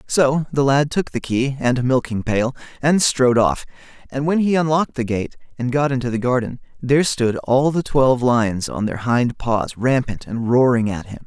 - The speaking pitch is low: Yes, low, 130 Hz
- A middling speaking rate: No, fast, 210 wpm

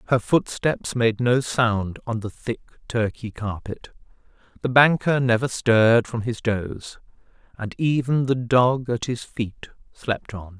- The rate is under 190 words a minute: Yes, average, 145 wpm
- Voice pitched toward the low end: Yes, low, 115 Hz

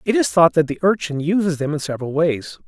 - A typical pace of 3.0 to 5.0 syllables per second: No, 6.1 syllables/s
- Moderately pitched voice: Yes, medium, 165 Hz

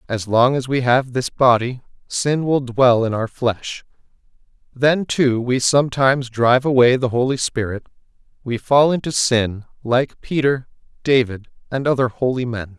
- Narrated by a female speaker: No, male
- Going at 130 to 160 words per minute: Yes, average, 155 wpm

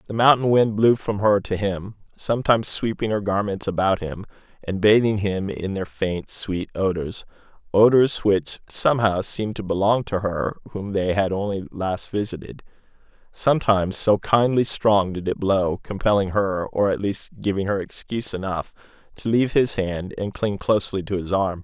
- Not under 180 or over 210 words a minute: No, average, 170 wpm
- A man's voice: Yes, male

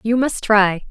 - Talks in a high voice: Yes, high, 220 Hz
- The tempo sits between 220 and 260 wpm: No, average, 200 wpm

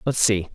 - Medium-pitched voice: No, low, 105 Hz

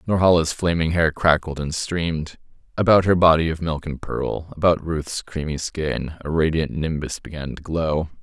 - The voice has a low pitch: Yes, very low, 80 Hz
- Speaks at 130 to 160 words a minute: Yes, average, 155 wpm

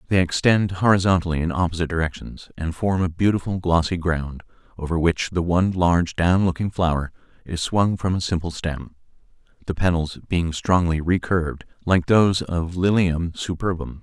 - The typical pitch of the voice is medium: No, very low, 85 Hz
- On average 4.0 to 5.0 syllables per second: No, 5.2 syllables/s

